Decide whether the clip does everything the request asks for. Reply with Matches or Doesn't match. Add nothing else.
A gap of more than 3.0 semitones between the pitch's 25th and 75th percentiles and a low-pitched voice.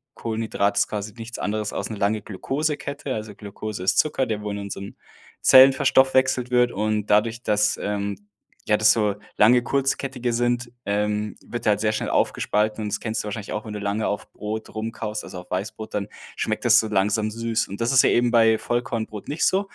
Doesn't match